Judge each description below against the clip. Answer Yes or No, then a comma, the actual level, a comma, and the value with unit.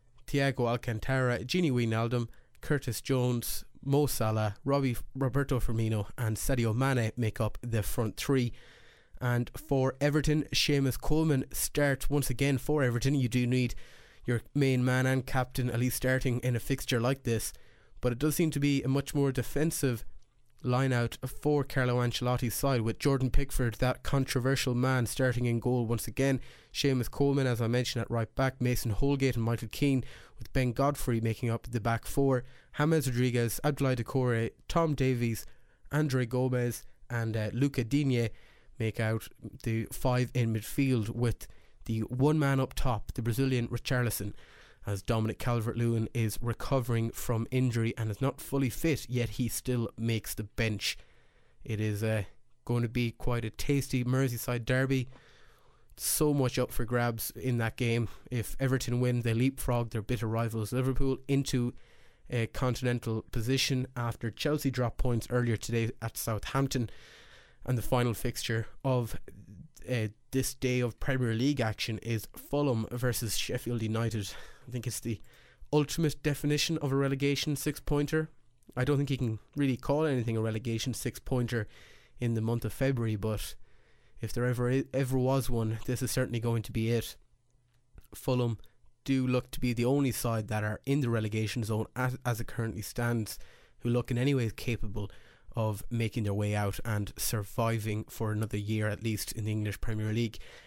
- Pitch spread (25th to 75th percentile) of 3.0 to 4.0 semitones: No, narrow, 2.6 semitones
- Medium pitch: No, low, 120 Hz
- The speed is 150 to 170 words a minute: Yes, average, 165 wpm